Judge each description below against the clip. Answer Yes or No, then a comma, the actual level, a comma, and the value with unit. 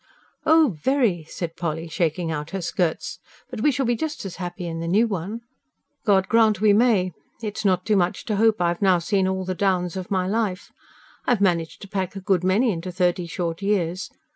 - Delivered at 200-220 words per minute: Yes, fast, 205 wpm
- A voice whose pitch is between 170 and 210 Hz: Yes, high, 190 Hz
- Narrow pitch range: No, average, 3.4 semitones